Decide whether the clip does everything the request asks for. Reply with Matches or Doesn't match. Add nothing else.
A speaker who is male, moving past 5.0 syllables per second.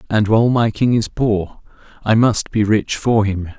Doesn't match